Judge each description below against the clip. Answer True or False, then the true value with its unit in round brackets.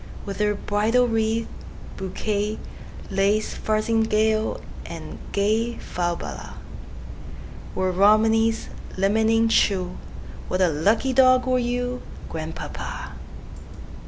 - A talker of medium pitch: False (215 Hz)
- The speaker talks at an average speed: False (70 wpm)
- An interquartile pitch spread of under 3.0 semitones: True (2.5 semitones)